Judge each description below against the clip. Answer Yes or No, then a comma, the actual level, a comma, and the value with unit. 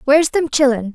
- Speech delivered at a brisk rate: No, average, 190 wpm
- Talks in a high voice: Yes, very high, 275 Hz